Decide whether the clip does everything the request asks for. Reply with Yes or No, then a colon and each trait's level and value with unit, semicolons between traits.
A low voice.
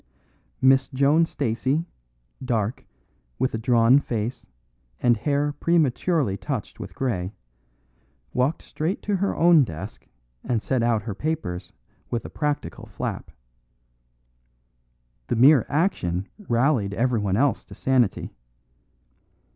Yes: low, 130 Hz